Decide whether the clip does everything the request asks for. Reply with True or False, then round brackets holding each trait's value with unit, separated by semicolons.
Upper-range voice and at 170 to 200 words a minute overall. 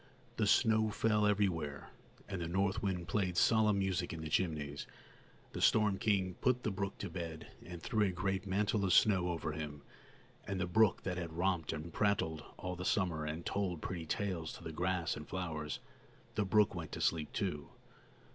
False (90 Hz; 185 wpm)